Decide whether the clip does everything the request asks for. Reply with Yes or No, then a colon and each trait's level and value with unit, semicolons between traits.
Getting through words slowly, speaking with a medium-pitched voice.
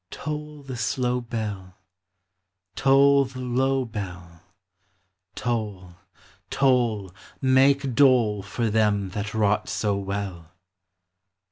No: slow, 95 wpm; low, 115 Hz